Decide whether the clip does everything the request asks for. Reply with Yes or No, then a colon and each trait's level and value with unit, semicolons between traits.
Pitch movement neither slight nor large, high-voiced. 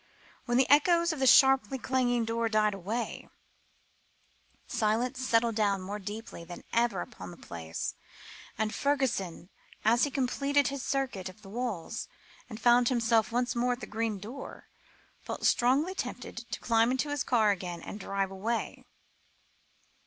Yes: average, 3.8 semitones; high, 235 Hz